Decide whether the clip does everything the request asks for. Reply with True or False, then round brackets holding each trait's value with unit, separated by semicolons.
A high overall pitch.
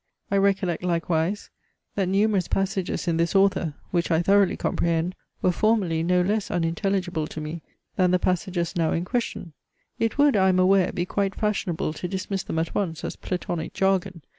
False (180 Hz)